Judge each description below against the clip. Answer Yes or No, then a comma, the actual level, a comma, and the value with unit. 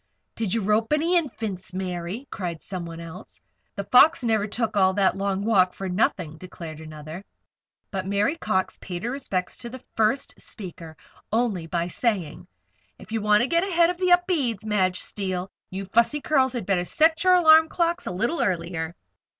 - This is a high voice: Yes, high, 205 Hz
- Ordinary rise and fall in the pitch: No, wide, 6.1 semitones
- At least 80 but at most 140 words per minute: No, average, 175 wpm